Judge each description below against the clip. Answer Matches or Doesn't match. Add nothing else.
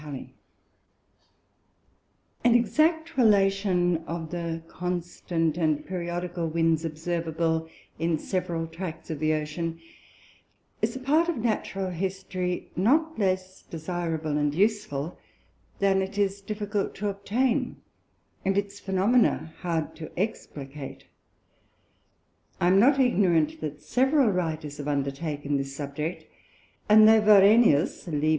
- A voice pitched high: Doesn't match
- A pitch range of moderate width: Matches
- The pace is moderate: Doesn't match